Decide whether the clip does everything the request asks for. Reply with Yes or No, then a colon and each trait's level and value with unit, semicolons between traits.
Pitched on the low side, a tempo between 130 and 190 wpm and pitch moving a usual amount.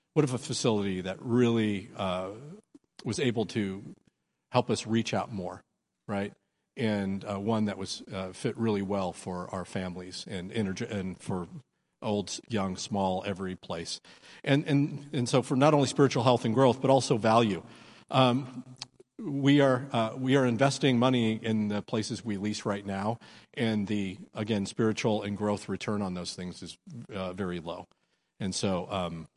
Yes: low, 110 Hz; average, 170 wpm; average, 4.4 semitones